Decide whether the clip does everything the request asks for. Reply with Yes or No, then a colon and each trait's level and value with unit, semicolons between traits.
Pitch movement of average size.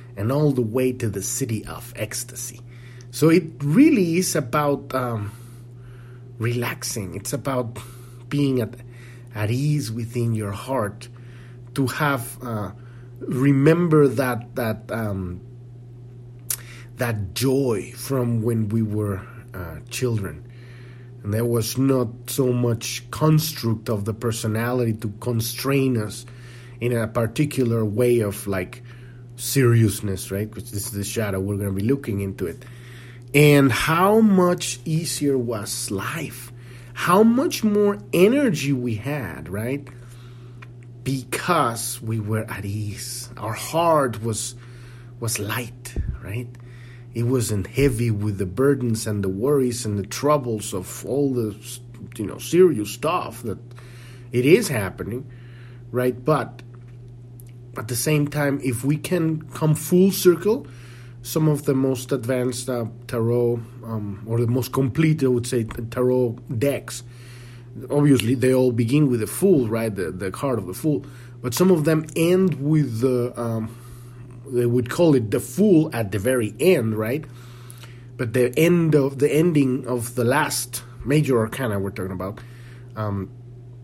No: narrow, 2.3 semitones